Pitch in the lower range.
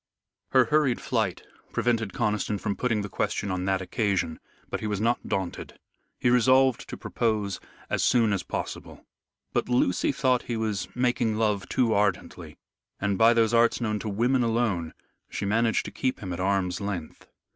Yes: low, 110 Hz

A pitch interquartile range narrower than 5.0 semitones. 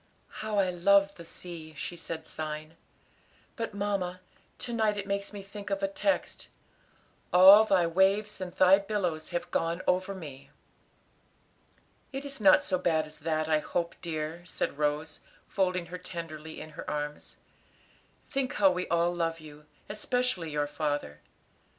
Yes: average, 4.0 semitones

